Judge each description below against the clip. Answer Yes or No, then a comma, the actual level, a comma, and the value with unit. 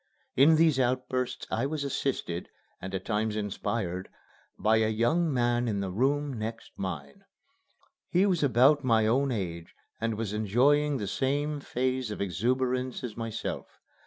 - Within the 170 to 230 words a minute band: No, average, 150 wpm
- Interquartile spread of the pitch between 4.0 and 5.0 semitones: Yes, average, 4.3 semitones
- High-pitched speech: No, low, 120 Hz